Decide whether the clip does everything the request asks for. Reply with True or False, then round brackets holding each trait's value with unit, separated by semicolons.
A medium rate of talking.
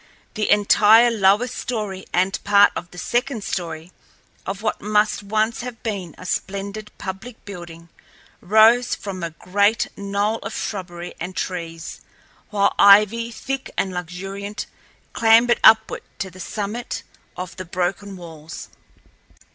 False (130 wpm)